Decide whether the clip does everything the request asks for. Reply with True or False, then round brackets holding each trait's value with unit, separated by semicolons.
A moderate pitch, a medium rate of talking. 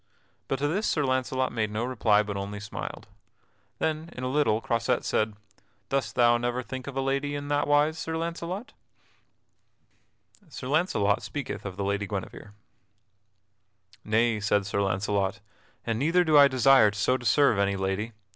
False (125 Hz; 165 wpm)